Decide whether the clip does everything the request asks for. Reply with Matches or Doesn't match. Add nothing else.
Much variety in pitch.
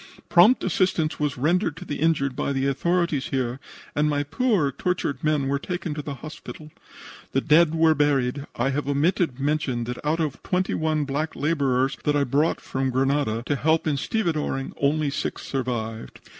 Doesn't match